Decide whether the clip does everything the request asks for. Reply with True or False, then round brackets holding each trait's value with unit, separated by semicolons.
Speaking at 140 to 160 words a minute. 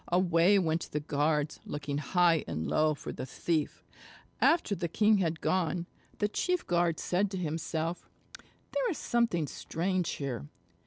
True (150 wpm)